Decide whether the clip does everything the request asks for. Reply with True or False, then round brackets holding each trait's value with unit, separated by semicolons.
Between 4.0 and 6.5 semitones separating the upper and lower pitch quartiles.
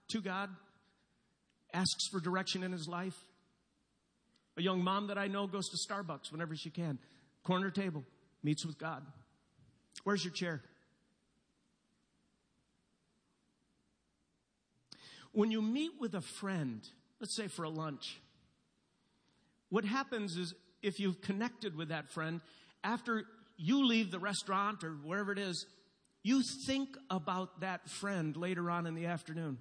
False (3.6 semitones)